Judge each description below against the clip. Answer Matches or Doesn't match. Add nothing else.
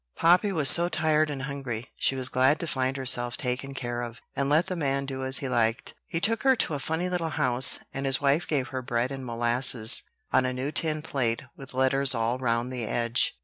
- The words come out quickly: Matches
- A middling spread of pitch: Matches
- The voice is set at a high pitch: Doesn't match